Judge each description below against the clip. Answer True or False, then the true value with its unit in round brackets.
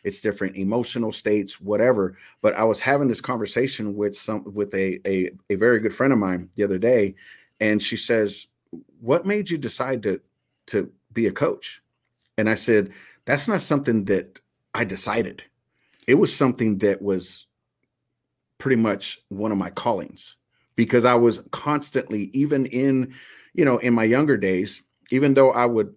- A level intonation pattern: False (4.2 semitones)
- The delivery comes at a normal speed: True (170 wpm)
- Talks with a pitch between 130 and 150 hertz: False (110 Hz)